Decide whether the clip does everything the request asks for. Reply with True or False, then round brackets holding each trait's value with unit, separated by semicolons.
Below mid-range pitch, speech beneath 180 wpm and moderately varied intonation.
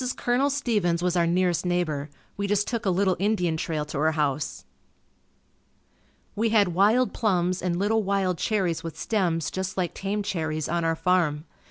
False (180 Hz; 170 wpm; 3.6 semitones)